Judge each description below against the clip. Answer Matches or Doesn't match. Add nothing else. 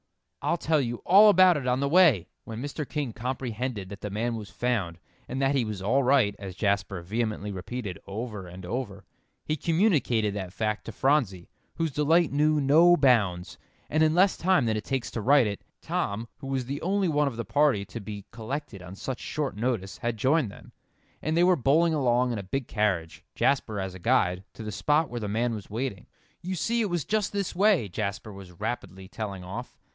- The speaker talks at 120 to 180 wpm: Doesn't match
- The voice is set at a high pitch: Doesn't match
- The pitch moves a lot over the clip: Matches